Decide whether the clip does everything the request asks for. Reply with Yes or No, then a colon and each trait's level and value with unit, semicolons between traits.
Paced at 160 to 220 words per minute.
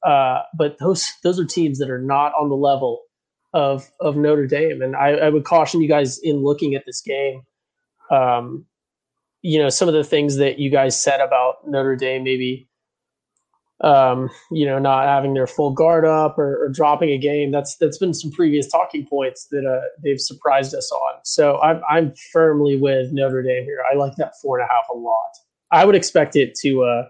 Yes: fast, 205 wpm